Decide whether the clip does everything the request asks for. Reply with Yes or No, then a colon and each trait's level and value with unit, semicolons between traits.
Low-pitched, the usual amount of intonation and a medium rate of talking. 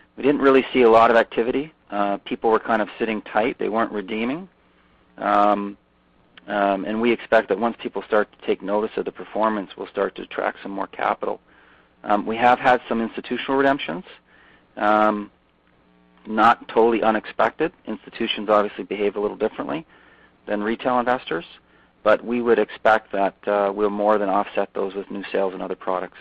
No: low, 105 Hz; narrow, 2.3 semitones; average, 175 wpm